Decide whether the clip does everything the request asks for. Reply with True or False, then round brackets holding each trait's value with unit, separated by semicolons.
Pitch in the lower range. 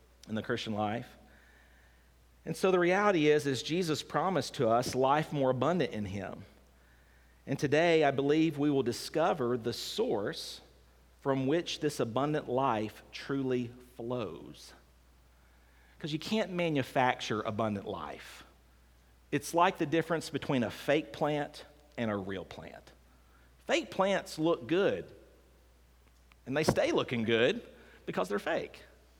True (120 Hz)